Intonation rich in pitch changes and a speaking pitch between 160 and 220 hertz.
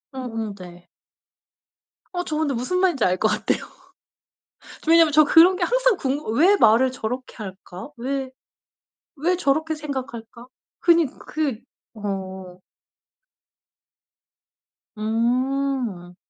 No: wide, 6.3 semitones; very high, 260 Hz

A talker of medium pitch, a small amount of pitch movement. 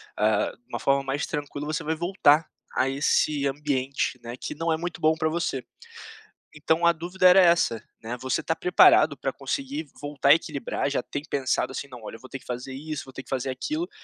No: medium, 145 Hz; average, 3.7 semitones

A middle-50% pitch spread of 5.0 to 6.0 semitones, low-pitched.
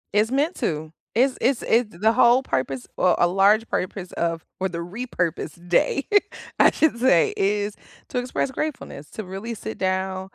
No: wide, 5.4 semitones; high, 205 Hz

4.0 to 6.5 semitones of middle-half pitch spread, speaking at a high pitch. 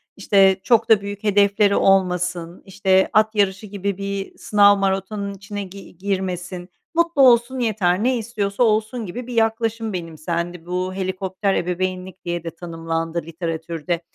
No: average, 2.9 semitones; high, 195 Hz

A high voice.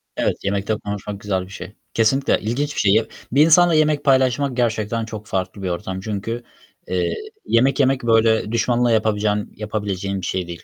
No: low, 110 Hz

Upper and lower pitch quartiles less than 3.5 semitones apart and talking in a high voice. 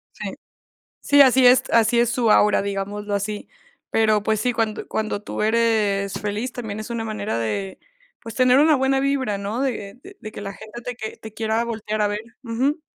Yes: average, 2.9 semitones; high, 220 Hz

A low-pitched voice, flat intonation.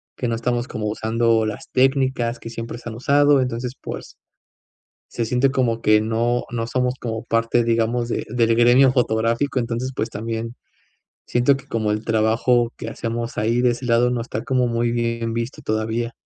Yes: low, 115 Hz; narrow, 1.4 semitones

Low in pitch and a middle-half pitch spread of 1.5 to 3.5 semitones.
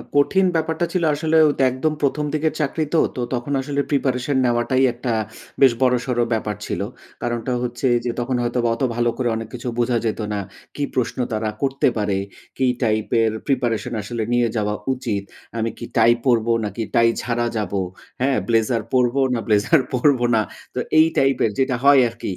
Yes: low, 125 Hz; average, 3.0 semitones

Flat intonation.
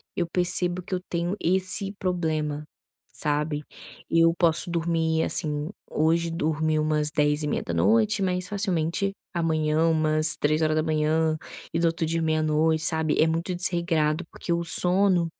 Yes: narrow, 1.9 semitones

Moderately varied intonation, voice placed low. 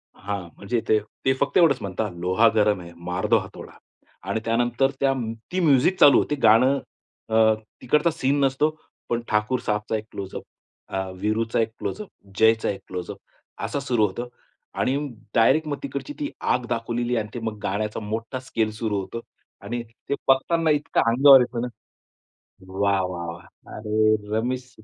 Yes: average, 4.0 semitones; low, 115 Hz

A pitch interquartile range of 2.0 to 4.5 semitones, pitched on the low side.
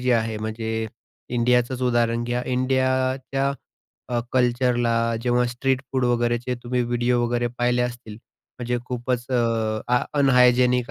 No: narrow, 1.0 semitones; low, 120 Hz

